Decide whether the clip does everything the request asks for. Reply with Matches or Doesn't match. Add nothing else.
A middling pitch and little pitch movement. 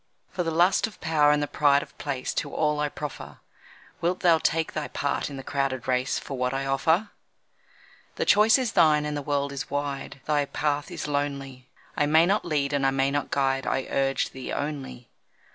Matches